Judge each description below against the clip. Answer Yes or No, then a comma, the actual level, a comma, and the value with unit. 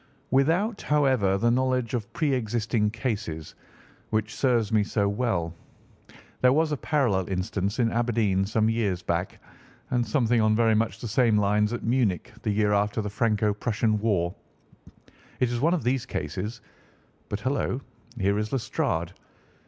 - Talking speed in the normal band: Yes, average, 150 wpm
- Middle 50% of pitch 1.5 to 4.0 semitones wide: Yes, average, 3.4 semitones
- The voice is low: Yes, low, 110 Hz